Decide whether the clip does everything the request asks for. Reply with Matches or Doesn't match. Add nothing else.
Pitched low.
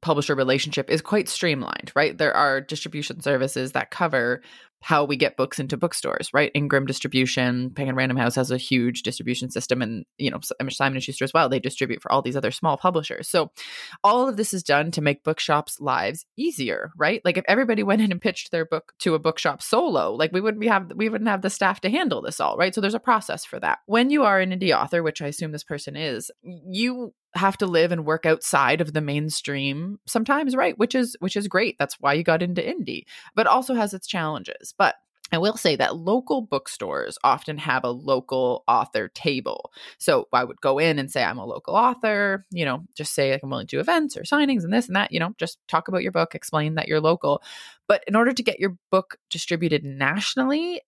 Doesn't match